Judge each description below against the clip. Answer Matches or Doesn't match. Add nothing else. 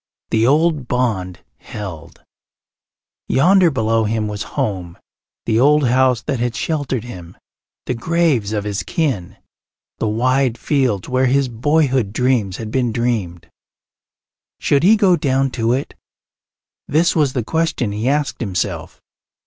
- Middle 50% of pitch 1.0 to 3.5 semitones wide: Doesn't match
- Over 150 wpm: Doesn't match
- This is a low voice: Matches